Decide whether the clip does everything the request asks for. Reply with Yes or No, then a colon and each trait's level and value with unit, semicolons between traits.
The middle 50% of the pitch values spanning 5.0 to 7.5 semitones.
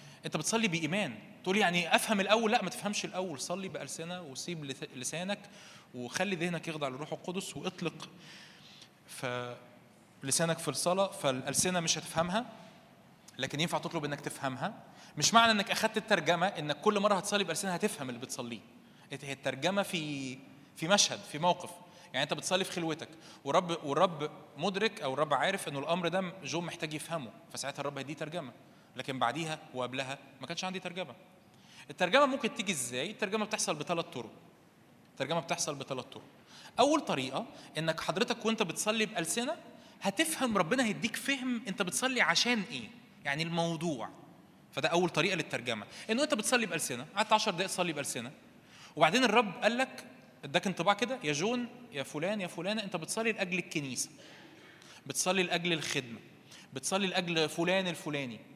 Yes: wide, 5.4 semitones